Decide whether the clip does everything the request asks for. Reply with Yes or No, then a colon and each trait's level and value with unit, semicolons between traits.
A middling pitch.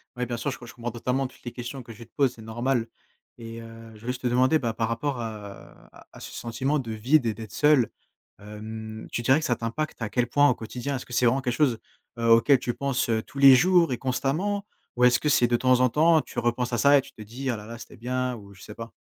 No: low, 120 Hz